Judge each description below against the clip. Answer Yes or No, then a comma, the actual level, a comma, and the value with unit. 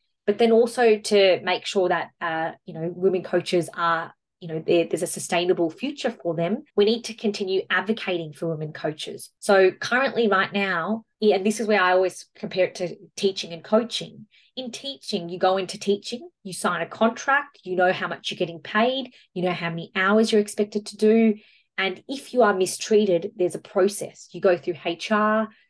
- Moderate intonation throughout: Yes, average, 3.4 semitones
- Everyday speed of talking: Yes, average, 195 wpm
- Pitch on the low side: No, high, 195 Hz